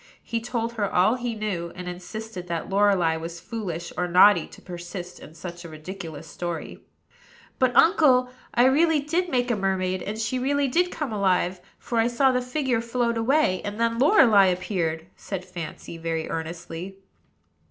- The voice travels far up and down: Yes, wide, 5.8 semitones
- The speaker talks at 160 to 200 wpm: Yes, average, 170 wpm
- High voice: Yes, high, 200 Hz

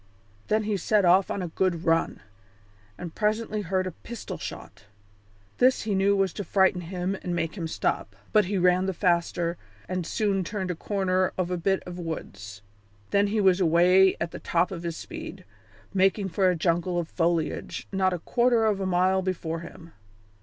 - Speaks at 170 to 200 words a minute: Yes, average, 190 wpm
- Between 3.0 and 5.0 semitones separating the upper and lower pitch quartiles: No, narrow, 2.4 semitones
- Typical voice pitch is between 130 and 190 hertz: Yes, medium, 185 Hz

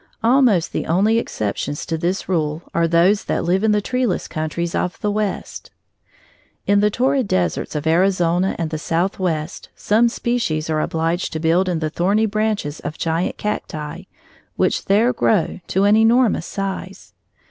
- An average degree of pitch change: Yes, average, 4.5 semitones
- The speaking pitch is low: No, medium, 185 Hz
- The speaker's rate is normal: Yes, average, 160 wpm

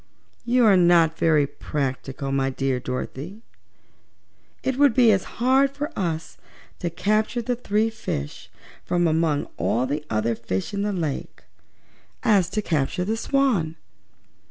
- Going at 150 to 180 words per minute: No, slow, 135 wpm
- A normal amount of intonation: No, wide, 7.6 semitones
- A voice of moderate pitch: Yes, medium, 175 Hz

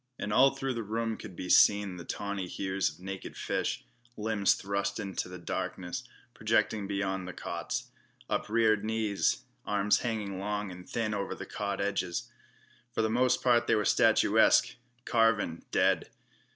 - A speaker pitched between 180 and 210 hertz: No, low, 100 Hz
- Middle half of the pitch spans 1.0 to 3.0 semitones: Yes, narrow, 2.6 semitones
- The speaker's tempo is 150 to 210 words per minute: Yes, average, 155 wpm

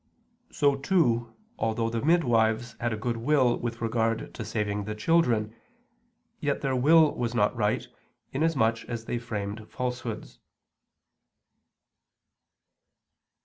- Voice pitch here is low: Yes, low, 115 Hz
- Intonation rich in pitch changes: No, narrow, 2.4 semitones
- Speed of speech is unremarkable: No, slow, 115 wpm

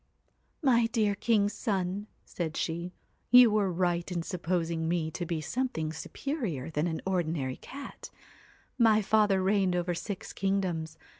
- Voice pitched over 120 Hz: Yes, medium, 185 Hz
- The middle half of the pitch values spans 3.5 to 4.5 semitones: Yes, average, 4.2 semitones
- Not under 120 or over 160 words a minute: Yes, average, 140 wpm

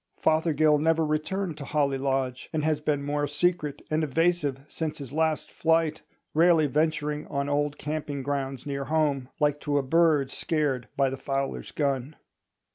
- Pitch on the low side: No, medium, 150 Hz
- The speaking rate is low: No, average, 160 wpm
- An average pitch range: No, narrow, 2.2 semitones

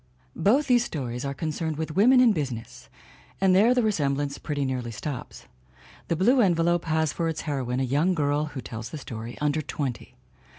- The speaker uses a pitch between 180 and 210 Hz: No, medium, 155 Hz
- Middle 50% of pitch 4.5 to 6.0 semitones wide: Yes, average, 5.0 semitones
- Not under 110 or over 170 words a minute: No, average, 185 wpm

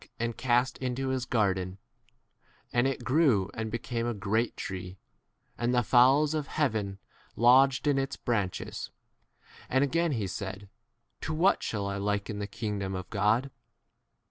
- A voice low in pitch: Yes, low, 115 Hz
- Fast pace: No, average, 155 wpm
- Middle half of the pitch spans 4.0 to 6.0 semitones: Yes, average, 4.7 semitones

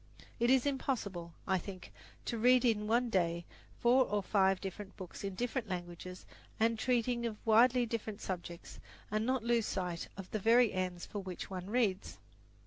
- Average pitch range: Yes, average, 4.2 semitones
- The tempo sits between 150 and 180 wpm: Yes, average, 170 wpm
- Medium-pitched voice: No, high, 210 Hz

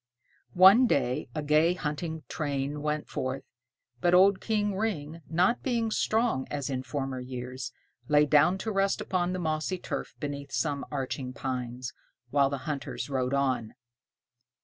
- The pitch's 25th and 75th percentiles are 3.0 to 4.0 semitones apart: No, average, 5.3 semitones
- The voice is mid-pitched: Yes, medium, 150 Hz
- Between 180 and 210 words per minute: No, average, 150 wpm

